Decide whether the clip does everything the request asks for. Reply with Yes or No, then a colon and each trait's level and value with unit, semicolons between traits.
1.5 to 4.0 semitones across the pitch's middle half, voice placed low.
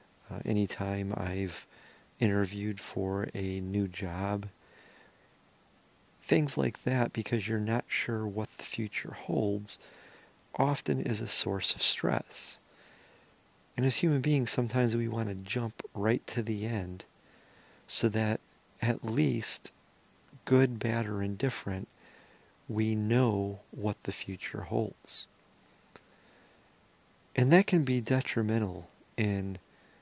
Yes: average, 3.2 semitones; low, 110 Hz